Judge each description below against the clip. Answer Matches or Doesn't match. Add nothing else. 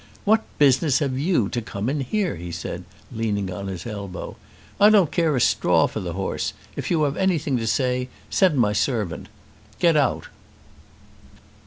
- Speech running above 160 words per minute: Matches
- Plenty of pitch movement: Matches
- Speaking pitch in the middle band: Doesn't match